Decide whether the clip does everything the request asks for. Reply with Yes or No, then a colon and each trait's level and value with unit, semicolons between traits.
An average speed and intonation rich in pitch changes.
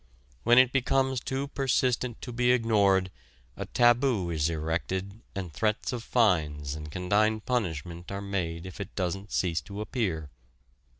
Yes: average, 145 wpm; wide, 5.9 semitones